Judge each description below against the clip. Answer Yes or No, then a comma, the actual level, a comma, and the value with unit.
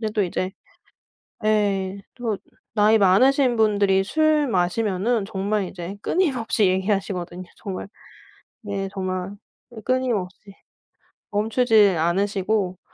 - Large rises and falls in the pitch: No, average, 2.8 semitones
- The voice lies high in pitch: Yes, high, 205 Hz